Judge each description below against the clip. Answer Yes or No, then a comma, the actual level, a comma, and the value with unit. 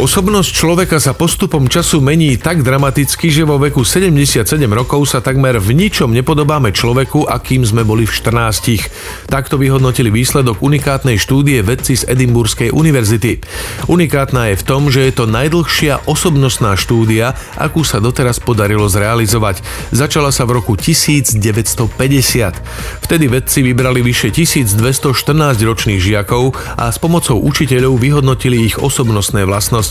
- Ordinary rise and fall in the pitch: Yes, average, 3.8 semitones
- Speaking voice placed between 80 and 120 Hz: No, low, 130 Hz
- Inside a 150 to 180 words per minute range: No, average, 135 wpm